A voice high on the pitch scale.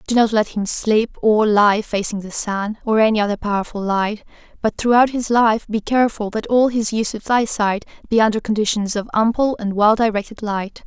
Yes: high, 215 Hz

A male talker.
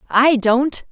No: female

